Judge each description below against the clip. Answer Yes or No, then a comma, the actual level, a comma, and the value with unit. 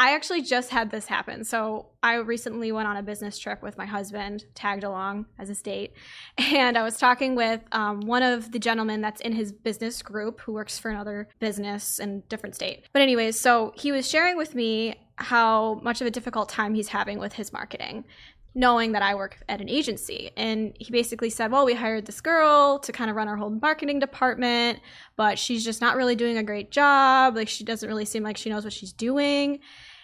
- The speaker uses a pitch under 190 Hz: No, high, 225 Hz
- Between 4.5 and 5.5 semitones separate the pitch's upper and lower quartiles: No, average, 2.7 semitones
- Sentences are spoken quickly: Yes, fast, 220 wpm